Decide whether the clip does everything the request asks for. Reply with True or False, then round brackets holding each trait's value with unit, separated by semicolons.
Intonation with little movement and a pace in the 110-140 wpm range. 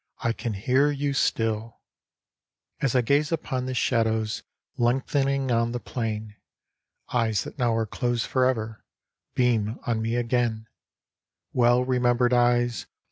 True (2.1 semitones; 135 wpm)